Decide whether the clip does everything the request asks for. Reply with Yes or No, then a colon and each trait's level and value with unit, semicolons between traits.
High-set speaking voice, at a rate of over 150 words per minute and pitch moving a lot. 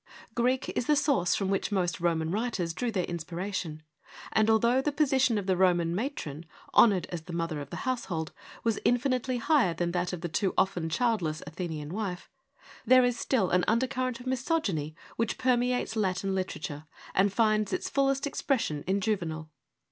Yes: high, 195 Hz; average, 170 wpm; wide, 6.3 semitones